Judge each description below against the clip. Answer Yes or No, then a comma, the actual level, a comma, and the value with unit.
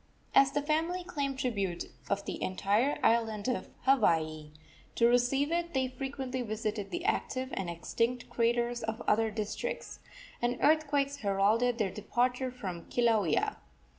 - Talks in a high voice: Yes, high, 240 Hz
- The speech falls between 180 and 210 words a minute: No, slow, 135 wpm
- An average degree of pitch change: Yes, average, 4.4 semitones